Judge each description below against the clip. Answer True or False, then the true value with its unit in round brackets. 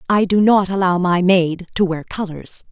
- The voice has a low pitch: False (185 Hz)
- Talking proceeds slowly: False (200 wpm)